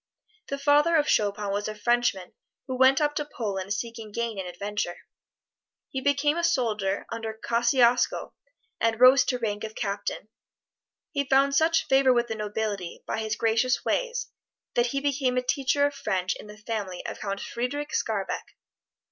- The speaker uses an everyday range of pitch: Yes, average, 4.7 semitones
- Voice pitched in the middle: No, high, 235 Hz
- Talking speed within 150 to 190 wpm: Yes, average, 165 wpm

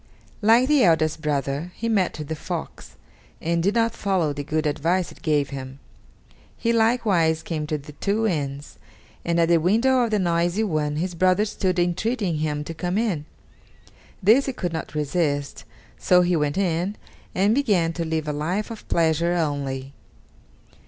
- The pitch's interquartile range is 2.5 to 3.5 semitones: No, average, 4.8 semitones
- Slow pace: No, average, 170 wpm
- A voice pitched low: No, medium, 170 Hz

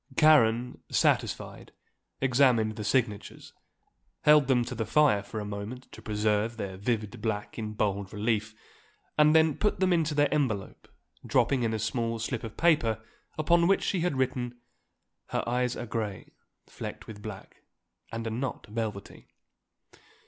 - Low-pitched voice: Yes, low, 115 Hz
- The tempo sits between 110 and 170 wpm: Yes, average, 150 wpm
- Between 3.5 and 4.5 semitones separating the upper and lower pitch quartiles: Yes, average, 4.1 semitones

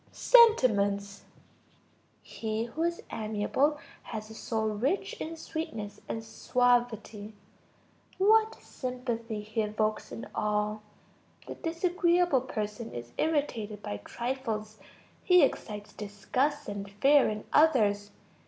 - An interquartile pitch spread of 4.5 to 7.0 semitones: Yes, wide, 5.6 semitones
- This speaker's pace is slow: Yes, slow, 105 wpm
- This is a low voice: No, high, 225 Hz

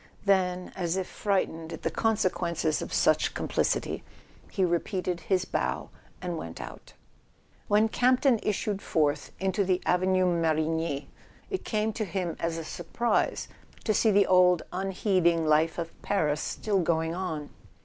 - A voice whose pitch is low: No, medium, 180 Hz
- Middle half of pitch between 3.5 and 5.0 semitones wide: No, average, 3.1 semitones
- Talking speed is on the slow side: No, average, 150 wpm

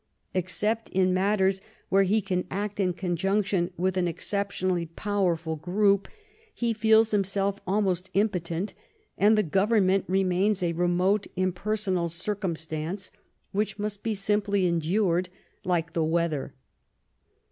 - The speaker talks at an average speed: No, slow, 120 wpm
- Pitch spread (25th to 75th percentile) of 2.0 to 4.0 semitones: Yes, average, 2.7 semitones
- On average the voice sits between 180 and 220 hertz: Yes, high, 190 Hz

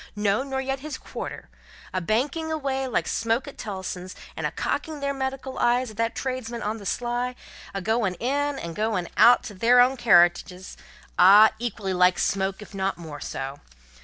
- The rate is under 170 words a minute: No, average, 180 wpm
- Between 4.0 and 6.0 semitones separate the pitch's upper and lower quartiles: Yes, wide, 5.6 semitones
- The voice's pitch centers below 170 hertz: No, high, 225 Hz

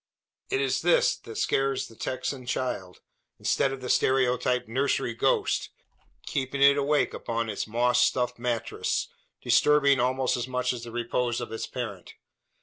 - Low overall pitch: Yes, low, 125 Hz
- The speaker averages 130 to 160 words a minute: Yes, average, 145 wpm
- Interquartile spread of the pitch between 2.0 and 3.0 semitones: Yes, narrow, 2.4 semitones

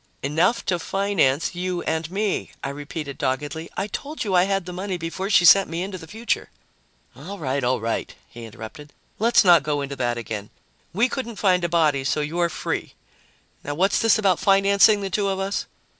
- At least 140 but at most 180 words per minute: No, average, 200 wpm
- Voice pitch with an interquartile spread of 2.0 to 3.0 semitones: No, average, 5.2 semitones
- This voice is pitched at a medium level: Yes, medium, 175 Hz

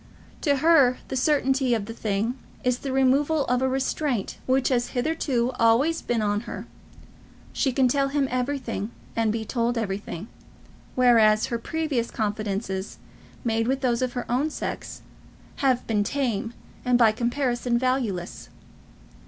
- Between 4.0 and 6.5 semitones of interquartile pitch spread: No, average, 2.9 semitones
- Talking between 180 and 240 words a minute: No, average, 145 wpm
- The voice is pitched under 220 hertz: No, high, 245 Hz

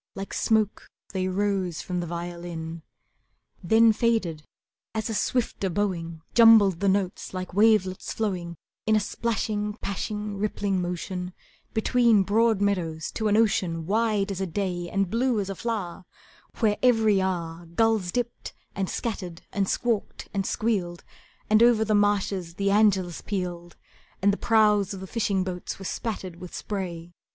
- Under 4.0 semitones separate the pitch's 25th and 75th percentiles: Yes, average, 3.3 semitones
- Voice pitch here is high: Yes, high, 195 Hz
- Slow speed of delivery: No, average, 150 wpm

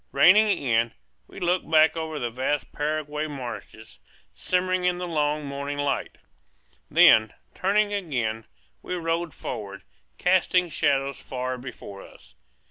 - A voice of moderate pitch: Yes, medium, 150 Hz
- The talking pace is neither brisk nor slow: No, slow, 125 wpm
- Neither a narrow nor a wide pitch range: No, wide, 5.7 semitones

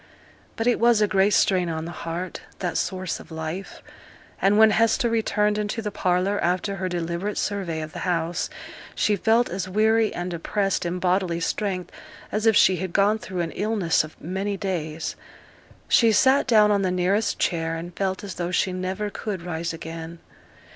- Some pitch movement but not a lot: Yes, average, 3.4 semitones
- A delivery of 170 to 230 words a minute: Yes, average, 180 wpm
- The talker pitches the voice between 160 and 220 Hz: Yes, medium, 185 Hz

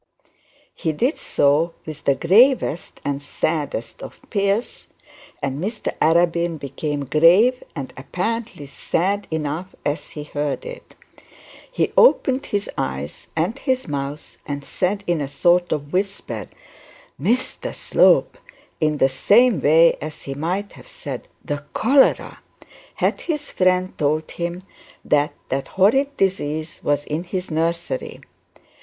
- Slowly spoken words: Yes, slow, 130 wpm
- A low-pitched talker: No, medium, 165 Hz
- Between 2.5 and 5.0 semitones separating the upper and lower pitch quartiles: No, wide, 5.5 semitones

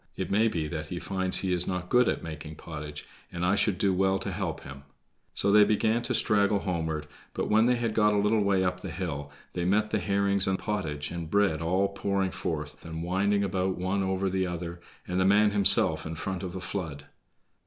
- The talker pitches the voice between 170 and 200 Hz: No, very low, 95 Hz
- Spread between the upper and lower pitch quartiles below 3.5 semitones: Yes, average, 3.1 semitones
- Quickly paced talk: Yes, fast, 220 wpm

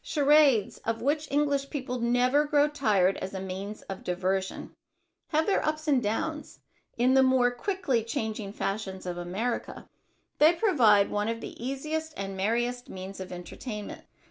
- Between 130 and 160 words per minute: Yes, average, 155 wpm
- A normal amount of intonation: No, wide, 6.6 semitones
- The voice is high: Yes, high, 240 Hz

